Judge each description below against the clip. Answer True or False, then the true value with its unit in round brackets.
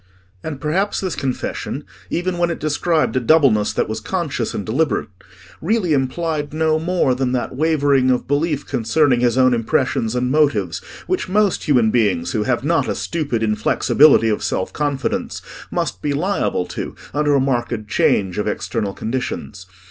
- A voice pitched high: False (135 Hz)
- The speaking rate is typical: True (165 wpm)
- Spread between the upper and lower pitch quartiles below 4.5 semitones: False (5.2 semitones)